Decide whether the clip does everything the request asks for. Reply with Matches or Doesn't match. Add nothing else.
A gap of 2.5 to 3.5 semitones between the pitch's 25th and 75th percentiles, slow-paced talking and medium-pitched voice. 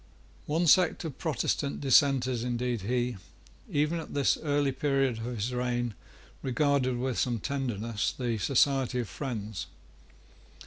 Doesn't match